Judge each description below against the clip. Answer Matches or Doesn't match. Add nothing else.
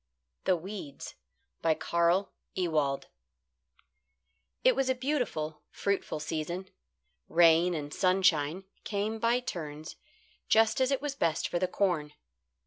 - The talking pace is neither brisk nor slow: Doesn't match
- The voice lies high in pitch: Doesn't match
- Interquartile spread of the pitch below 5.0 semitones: Doesn't match